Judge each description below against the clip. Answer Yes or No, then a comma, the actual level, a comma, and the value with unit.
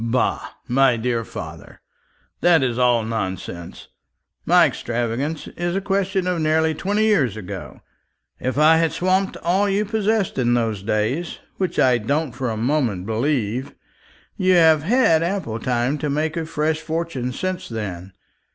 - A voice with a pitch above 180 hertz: No, medium, 150 Hz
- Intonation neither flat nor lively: No, wide, 6.7 semitones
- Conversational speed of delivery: Yes, average, 150 wpm